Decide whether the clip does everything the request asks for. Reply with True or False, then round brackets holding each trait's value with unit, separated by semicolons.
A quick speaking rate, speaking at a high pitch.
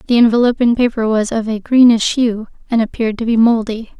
False (195 wpm; 230 Hz)